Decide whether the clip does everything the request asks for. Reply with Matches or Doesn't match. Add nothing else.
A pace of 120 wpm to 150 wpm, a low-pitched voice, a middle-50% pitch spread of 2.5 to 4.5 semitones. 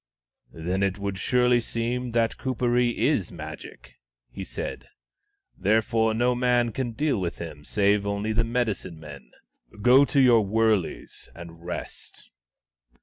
Matches